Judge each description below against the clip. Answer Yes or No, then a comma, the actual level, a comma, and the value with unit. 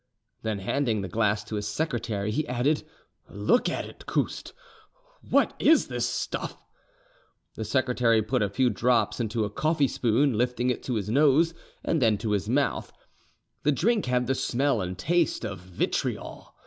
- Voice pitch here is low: Yes, low, 120 Hz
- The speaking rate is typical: Yes, average, 165 wpm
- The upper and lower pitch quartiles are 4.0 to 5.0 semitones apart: Yes, average, 4.7 semitones